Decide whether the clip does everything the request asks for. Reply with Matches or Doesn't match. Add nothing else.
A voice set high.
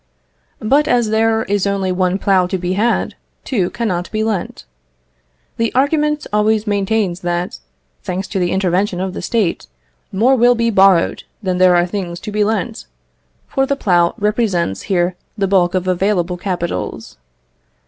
Matches